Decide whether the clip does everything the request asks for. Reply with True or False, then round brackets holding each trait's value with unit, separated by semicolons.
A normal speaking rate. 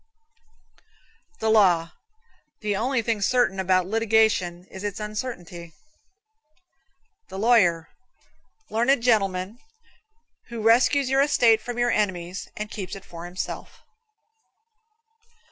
False (105 wpm)